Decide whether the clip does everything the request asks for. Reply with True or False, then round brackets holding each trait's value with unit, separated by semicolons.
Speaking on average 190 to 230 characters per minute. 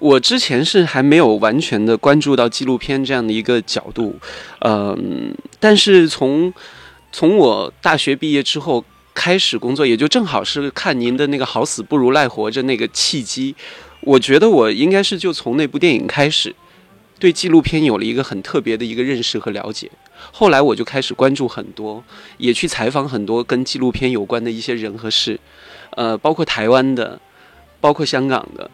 False (280 characters per minute)